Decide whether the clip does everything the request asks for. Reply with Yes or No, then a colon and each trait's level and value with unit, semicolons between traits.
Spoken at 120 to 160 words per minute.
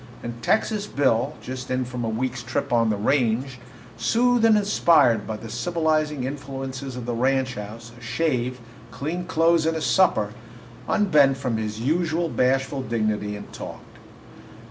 Yes: average, 155 wpm